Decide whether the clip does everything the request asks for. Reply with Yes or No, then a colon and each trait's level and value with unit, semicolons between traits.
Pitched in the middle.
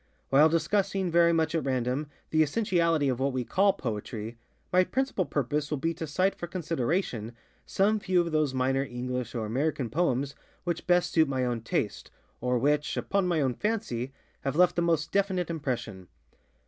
Yes: medium, 150 Hz